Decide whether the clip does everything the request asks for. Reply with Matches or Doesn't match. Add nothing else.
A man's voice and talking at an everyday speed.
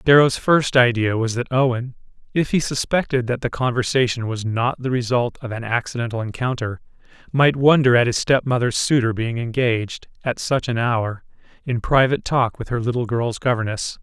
Matches